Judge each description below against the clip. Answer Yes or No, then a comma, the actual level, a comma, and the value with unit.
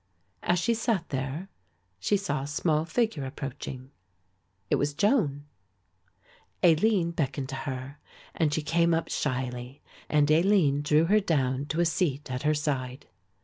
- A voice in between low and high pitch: Yes, medium, 150 Hz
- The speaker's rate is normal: Yes, average, 145 wpm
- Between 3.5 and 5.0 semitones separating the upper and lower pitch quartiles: Yes, average, 4.0 semitones